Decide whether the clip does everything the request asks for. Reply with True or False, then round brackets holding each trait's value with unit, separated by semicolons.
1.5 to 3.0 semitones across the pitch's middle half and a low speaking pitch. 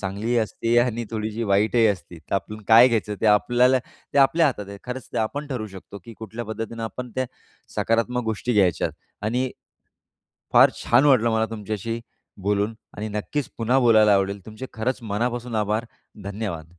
True (2.7 semitones; 110 Hz)